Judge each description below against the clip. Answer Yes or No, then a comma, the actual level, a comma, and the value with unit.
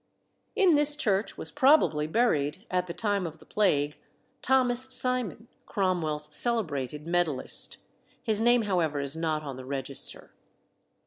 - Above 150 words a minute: No, slow, 135 wpm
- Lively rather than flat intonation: Yes, wide, 7.9 semitones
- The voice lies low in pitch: No, medium, 180 Hz